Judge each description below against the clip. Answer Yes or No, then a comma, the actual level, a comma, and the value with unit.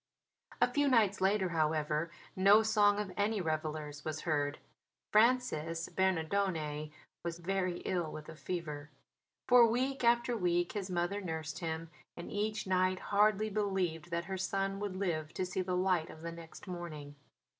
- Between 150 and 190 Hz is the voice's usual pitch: Yes, medium, 185 Hz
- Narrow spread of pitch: No, average, 4.1 semitones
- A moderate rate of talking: Yes, average, 155 wpm